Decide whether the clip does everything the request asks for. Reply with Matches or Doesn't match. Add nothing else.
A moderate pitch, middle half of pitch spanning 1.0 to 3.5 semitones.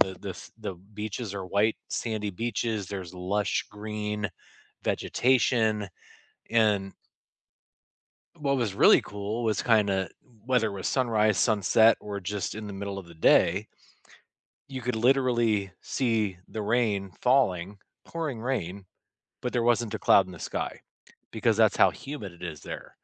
Doesn't match